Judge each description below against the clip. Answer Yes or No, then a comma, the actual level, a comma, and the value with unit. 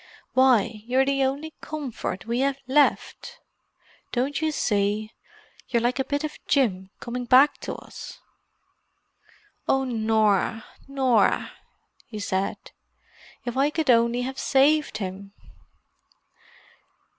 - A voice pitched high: Yes, very high, 250 Hz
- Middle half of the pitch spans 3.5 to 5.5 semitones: Yes, average, 4.0 semitones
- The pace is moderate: No, slow, 110 wpm